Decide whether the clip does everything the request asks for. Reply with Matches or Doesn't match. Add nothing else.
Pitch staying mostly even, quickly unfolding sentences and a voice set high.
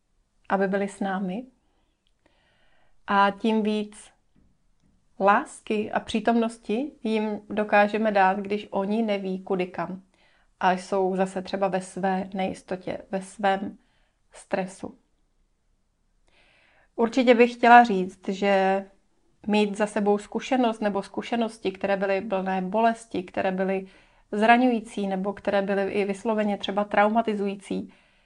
Doesn't match